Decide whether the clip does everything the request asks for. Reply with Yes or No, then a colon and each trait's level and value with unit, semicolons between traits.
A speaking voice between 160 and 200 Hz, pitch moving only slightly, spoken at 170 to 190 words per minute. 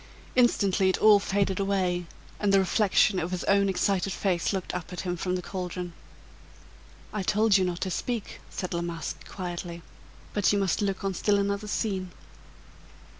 Yes: high, 190 Hz; narrow, 1.9 semitones; average, 175 wpm